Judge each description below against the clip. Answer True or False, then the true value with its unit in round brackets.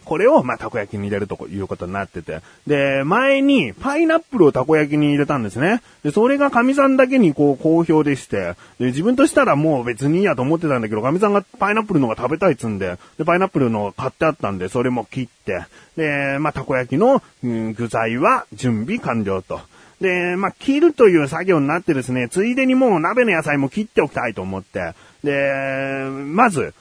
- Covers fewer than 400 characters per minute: False (410 characters per minute)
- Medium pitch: True (145 Hz)